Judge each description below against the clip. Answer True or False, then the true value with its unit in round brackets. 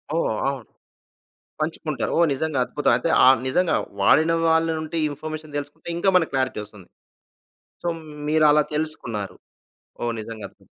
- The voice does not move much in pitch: False (3.8 semitones)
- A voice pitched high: False (150 Hz)